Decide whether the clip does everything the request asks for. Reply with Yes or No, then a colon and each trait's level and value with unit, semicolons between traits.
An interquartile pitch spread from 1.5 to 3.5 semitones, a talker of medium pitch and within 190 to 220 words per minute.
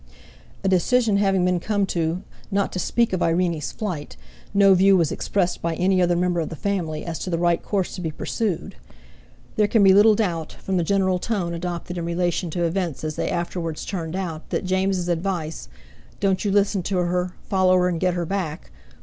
Yes: narrow, 2.4 semitones; medium, 180 Hz; average, 200 wpm